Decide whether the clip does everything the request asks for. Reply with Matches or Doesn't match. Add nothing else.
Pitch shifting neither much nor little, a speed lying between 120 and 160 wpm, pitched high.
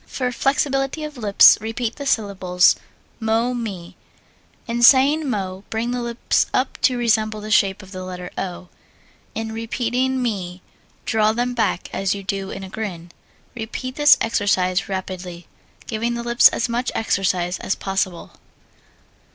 Matches